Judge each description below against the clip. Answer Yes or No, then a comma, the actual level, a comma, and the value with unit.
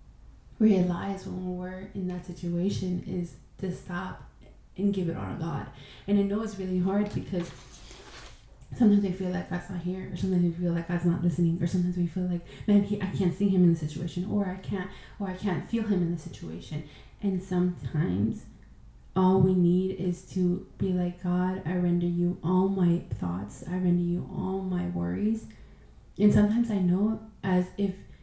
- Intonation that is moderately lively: No, narrow, 1.6 semitones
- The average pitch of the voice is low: No, medium, 180 Hz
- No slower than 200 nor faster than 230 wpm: No, average, 190 wpm